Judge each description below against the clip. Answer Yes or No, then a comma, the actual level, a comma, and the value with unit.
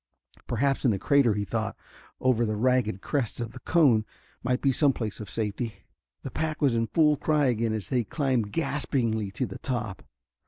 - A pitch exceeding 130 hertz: No, low, 120 Hz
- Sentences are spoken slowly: No, average, 190 wpm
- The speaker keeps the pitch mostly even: No, average, 4.1 semitones